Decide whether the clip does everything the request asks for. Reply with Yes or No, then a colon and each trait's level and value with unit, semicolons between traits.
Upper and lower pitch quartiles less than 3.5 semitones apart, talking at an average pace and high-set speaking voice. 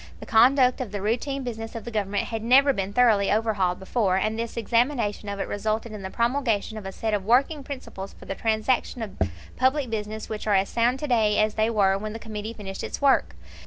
No: average, 2.9 semitones; fast, 225 wpm; high, 220 Hz